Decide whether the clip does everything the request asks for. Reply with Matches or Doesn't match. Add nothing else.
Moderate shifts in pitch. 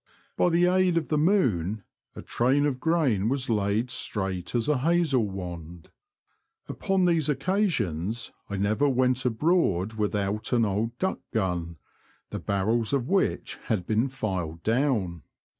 Doesn't match